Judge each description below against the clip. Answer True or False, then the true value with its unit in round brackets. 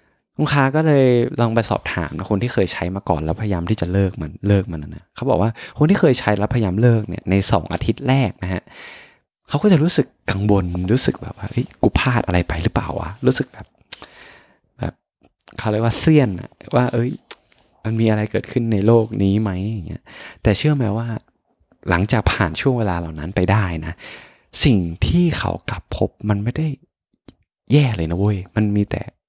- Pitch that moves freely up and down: False (4.8 semitones)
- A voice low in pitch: True (105 Hz)